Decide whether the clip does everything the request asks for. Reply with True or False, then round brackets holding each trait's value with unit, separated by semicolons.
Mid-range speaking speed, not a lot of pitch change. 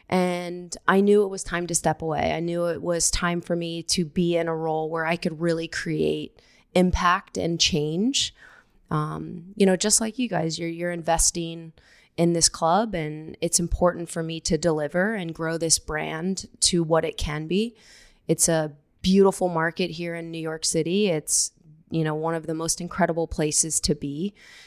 True (190 wpm; 1.7 semitones)